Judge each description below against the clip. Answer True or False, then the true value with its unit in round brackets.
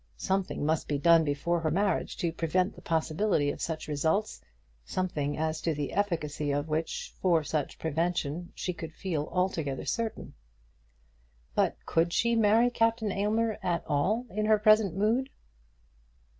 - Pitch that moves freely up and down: False (4.9 semitones)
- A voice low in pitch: False (170 Hz)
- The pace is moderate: True (150 wpm)